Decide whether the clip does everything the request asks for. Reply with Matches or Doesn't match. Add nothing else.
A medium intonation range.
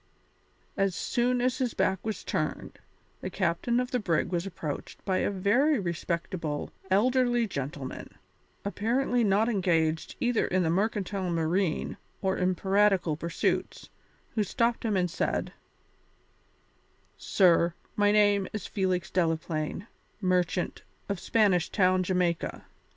Matches